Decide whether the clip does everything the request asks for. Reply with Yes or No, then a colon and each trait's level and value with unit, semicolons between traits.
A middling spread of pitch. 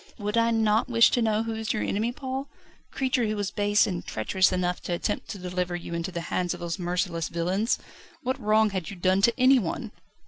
Yes: average, 4.2 semitones